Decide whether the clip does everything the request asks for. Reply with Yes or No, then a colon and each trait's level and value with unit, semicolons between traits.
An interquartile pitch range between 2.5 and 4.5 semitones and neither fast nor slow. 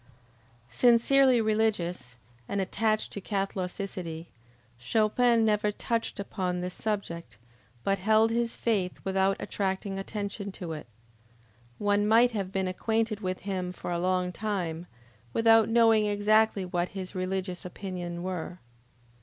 No: average, 3.1 semitones; slow, 125 wpm